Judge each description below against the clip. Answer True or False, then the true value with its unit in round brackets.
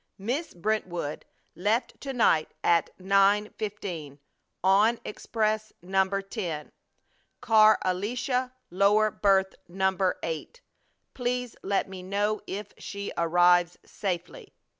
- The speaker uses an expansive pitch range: False (3.0 semitones)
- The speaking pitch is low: False (200 Hz)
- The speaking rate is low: True (105 wpm)